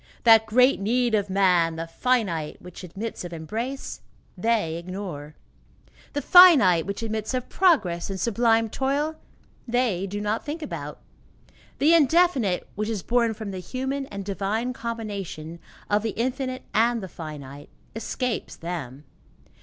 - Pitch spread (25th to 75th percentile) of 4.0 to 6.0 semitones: Yes, wide, 5.6 semitones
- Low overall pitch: No, high, 215 Hz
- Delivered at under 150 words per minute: Yes, average, 140 wpm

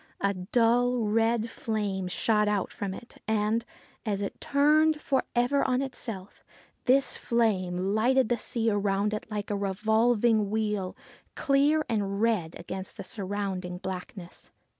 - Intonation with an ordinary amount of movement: Yes, average, 3.3 semitones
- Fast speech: No, slow, 135 wpm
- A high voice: Yes, high, 215 Hz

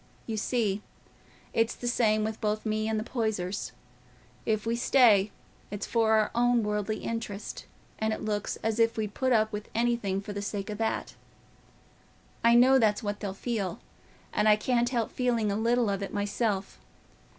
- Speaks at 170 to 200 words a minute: Yes, average, 175 wpm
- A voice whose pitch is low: No, high, 220 Hz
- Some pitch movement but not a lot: No, narrow, 2.1 semitones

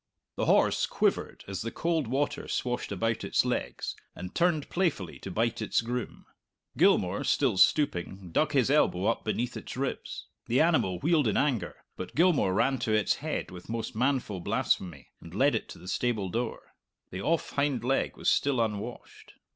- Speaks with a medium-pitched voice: No, low, 120 Hz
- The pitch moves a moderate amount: No, wide, 6.0 semitones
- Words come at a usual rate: Yes, average, 175 wpm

